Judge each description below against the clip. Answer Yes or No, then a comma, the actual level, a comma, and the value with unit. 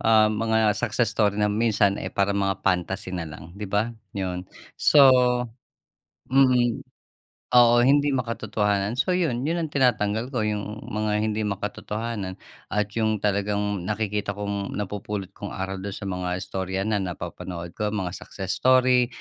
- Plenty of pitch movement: No, narrow, 2.5 semitones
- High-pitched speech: No, low, 105 Hz